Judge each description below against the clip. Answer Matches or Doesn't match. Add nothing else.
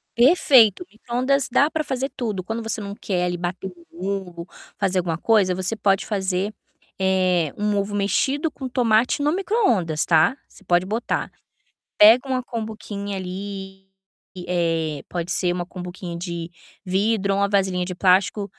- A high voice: Matches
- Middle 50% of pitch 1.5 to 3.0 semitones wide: Doesn't match